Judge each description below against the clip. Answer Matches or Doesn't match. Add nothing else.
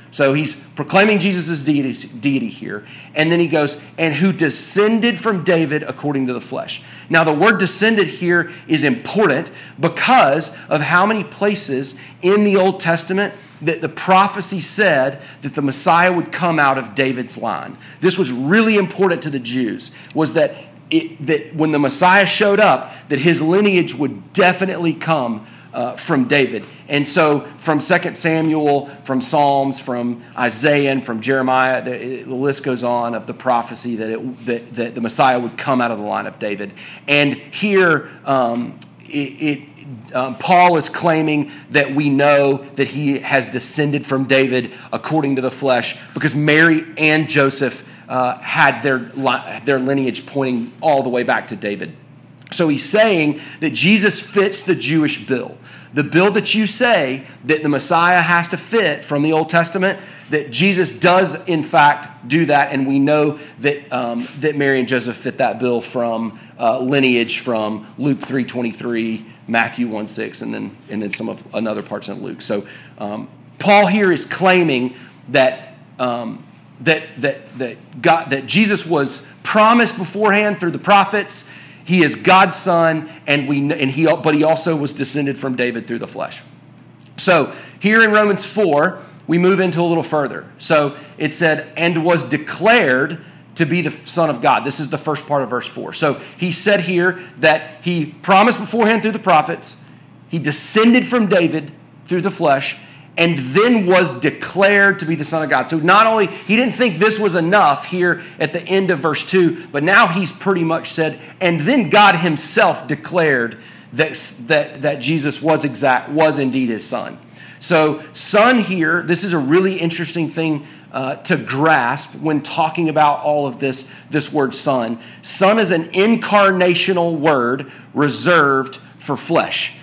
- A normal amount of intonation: Matches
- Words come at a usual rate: Matches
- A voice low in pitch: Doesn't match